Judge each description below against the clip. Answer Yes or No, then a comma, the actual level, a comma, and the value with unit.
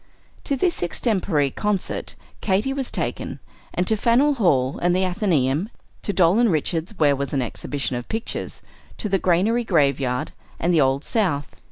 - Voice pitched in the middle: Yes, medium, 180 Hz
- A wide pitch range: Yes, wide, 7.1 semitones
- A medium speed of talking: Yes, average, 165 wpm